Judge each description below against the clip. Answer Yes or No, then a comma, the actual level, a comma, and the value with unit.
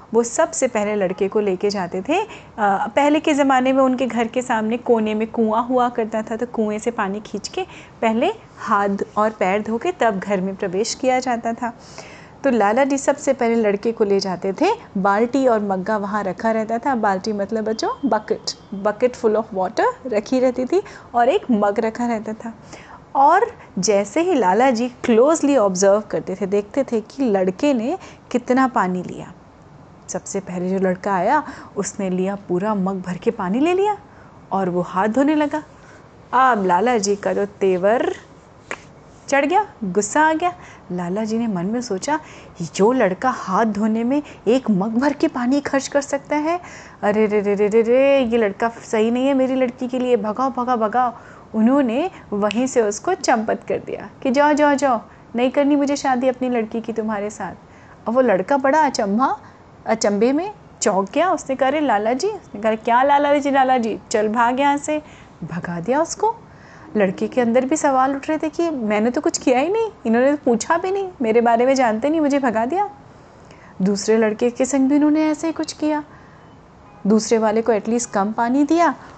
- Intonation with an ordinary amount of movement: Yes, average, 4.9 semitones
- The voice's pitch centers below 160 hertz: No, high, 235 Hz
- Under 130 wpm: No, fast, 190 wpm